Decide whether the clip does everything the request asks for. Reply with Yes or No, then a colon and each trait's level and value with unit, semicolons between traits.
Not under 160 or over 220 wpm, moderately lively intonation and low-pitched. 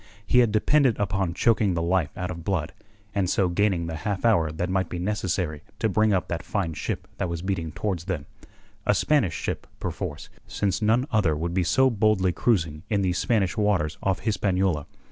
Yes: average, 195 wpm; average, 3.7 semitones; very low, 95 Hz